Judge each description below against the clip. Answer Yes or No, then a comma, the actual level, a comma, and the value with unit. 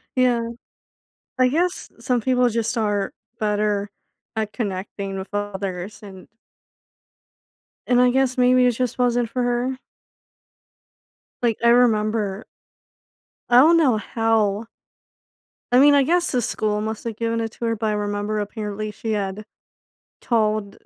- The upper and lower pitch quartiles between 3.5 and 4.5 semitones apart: No, average, 3.0 semitones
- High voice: Yes, high, 225 Hz